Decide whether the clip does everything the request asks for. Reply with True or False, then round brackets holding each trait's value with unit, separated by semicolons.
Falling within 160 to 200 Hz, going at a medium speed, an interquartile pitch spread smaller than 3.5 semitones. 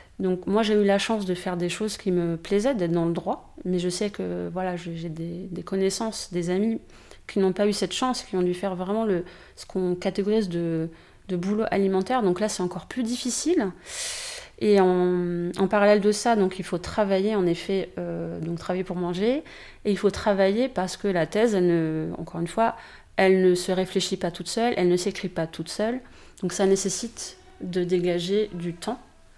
True (190 Hz; 210 wpm; 2.9 semitones)